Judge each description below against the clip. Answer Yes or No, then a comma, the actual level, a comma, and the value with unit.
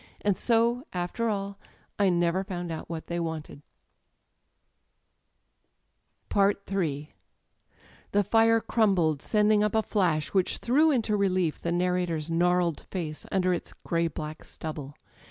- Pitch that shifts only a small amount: No, average, 3.8 semitones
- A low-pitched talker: No, medium, 180 Hz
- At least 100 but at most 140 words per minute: Yes, slow, 135 wpm